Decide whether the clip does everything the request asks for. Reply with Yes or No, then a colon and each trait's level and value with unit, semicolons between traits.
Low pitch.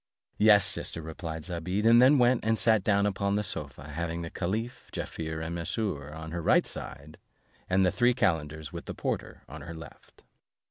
Yes: very low, 90 Hz